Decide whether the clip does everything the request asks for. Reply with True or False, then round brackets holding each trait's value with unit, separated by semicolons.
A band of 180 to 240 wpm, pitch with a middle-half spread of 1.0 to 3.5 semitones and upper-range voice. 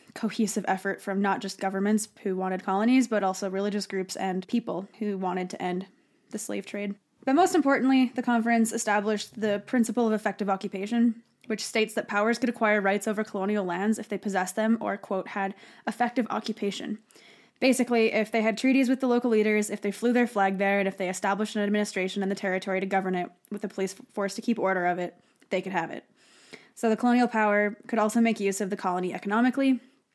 True (205 wpm; 2.9 semitones; 210 Hz)